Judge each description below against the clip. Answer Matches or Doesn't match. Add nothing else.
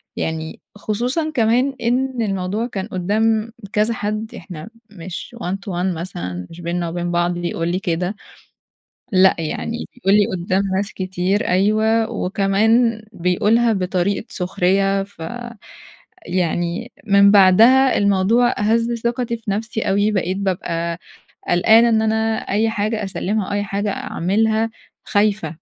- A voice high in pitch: Matches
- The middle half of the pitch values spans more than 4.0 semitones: Doesn't match